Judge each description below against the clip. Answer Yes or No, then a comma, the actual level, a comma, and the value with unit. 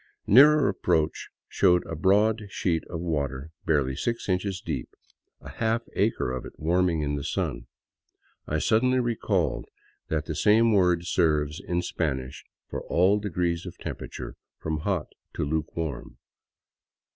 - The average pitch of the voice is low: Yes, very low, 85 Hz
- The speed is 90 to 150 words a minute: Yes, average, 145 wpm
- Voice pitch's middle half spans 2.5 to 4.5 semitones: No, average, 4.9 semitones